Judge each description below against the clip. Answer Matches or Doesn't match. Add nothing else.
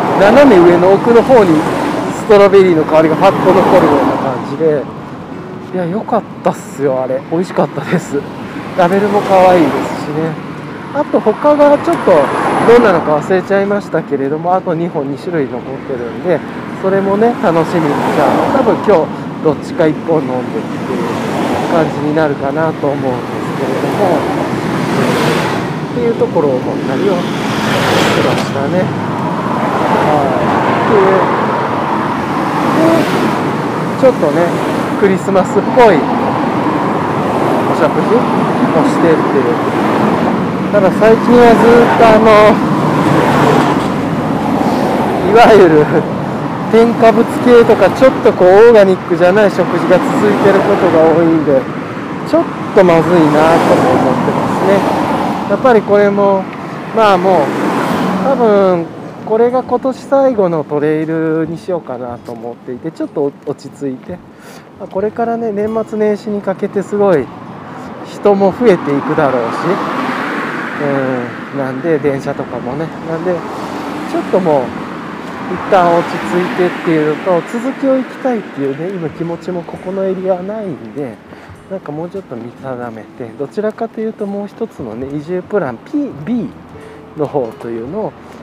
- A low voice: Doesn't match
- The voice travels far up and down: Matches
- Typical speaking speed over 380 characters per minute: Doesn't match